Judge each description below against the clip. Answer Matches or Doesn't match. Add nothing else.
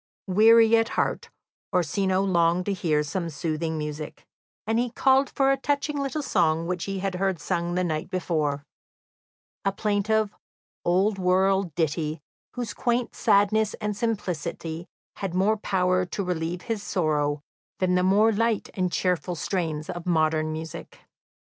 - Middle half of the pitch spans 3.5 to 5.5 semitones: Matches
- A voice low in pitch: Doesn't match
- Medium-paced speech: Matches